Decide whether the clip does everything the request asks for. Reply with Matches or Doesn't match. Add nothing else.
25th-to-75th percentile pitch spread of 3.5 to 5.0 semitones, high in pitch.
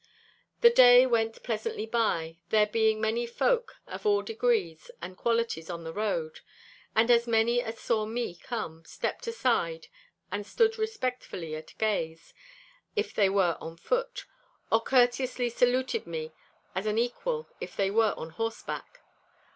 Matches